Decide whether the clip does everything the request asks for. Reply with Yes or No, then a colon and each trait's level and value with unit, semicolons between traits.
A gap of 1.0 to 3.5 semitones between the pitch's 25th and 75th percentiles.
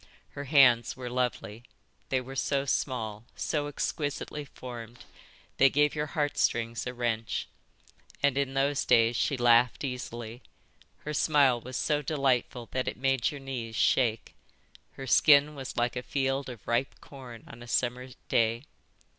Yes: average, 2.9 semitones